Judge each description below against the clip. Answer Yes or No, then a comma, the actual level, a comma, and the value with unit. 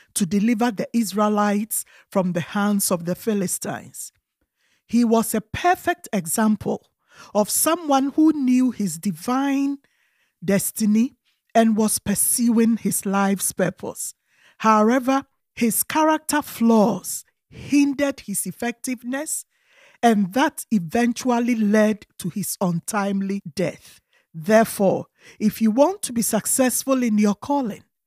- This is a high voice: Yes, high, 225 Hz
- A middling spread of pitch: Yes, average, 4.5 semitones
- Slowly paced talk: Yes, slow, 115 wpm